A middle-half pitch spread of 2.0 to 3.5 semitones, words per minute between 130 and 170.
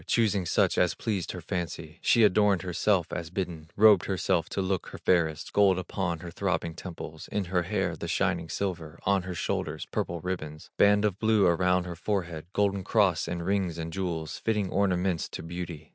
No: average, 2.8 semitones; average, 185 wpm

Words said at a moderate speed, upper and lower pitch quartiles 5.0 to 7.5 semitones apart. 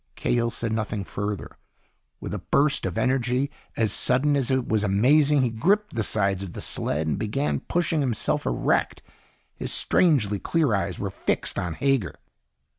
Yes: average, 165 wpm; wide, 5.6 semitones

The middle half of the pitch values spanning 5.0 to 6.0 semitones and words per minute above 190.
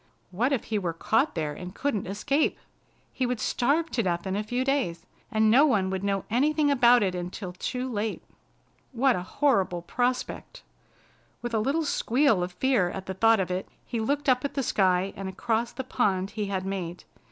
Yes: wide, 5.4 semitones; average, 200 wpm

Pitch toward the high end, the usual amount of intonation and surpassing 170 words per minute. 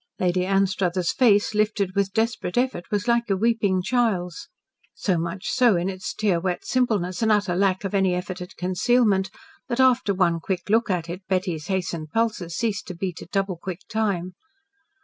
Yes: high, 195 Hz; average, 3.2 semitones; average, 180 wpm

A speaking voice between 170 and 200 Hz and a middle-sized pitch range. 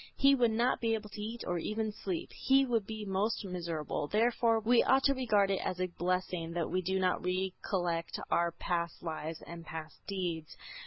Yes: high, 190 Hz; average, 4.5 semitones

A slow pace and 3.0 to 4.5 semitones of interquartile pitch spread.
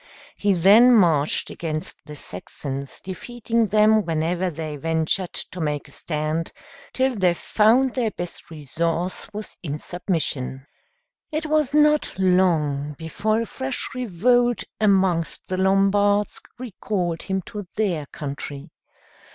No: slow, 125 wpm; average, 5.3 semitones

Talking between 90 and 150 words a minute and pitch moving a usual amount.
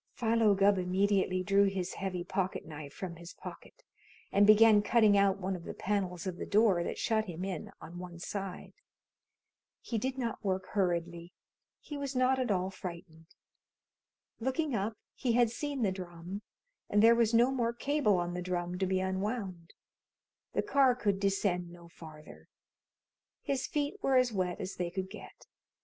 No: average, 170 wpm; average, 4.2 semitones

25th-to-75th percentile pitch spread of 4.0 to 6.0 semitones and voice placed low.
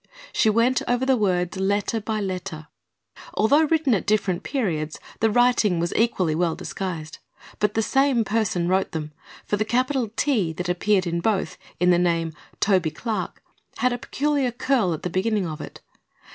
No: average, 5.2 semitones; high, 205 Hz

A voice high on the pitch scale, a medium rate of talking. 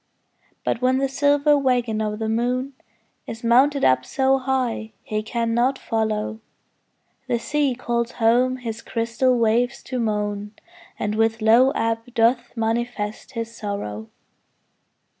No: high, 235 Hz; slow, 130 wpm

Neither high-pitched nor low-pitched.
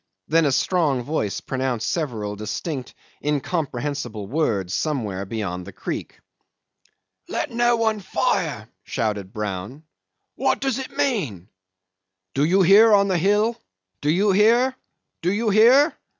Yes: medium, 155 Hz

